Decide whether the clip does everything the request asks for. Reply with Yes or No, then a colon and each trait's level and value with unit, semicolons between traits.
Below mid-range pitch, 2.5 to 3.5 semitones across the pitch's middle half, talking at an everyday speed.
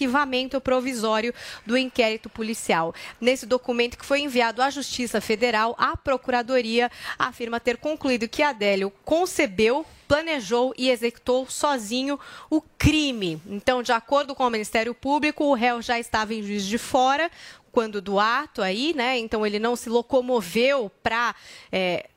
No: high, 245 Hz; average, 3.0 semitones; average, 145 wpm